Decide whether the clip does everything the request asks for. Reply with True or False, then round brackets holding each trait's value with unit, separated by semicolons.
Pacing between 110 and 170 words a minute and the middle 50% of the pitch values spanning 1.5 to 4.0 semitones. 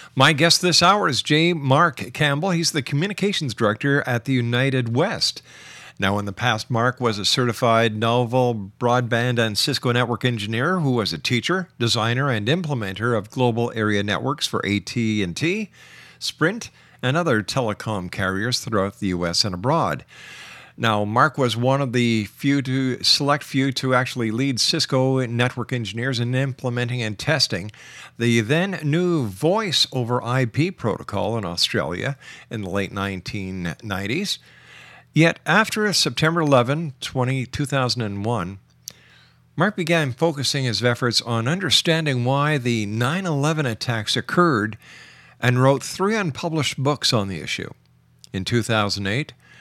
False (140 wpm; 4.7 semitones)